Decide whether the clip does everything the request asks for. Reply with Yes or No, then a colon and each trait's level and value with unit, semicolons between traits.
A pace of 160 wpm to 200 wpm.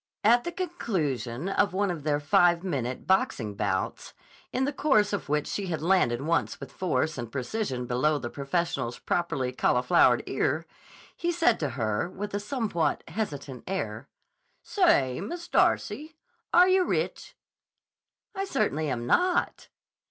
No: average, 145 wpm